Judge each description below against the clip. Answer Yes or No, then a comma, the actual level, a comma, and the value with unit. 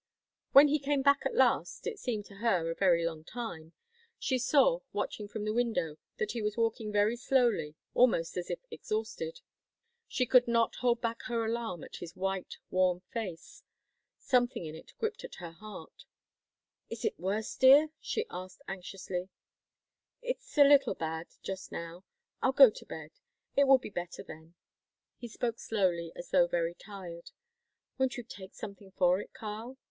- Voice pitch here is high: Yes, high, 215 Hz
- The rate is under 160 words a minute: No, average, 170 wpm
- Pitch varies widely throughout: Yes, wide, 6.0 semitones